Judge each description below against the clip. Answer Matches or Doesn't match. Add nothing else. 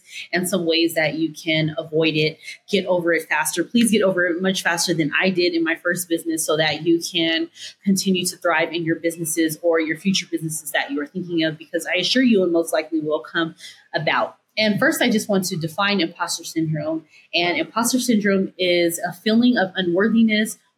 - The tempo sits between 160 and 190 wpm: Doesn't match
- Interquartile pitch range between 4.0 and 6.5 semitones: Doesn't match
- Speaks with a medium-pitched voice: Matches